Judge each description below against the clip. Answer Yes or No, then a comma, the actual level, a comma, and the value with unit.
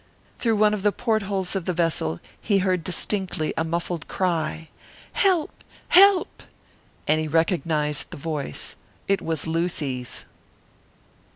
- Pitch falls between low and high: Yes, medium, 170 Hz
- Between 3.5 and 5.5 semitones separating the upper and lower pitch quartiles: Yes, average, 4.0 semitones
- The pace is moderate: No, slow, 125 wpm